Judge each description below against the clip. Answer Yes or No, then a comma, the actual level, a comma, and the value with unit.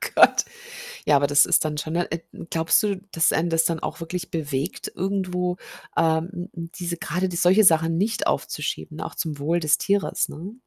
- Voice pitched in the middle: Yes, medium, 170 Hz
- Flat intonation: Yes, narrow, 2.2 semitones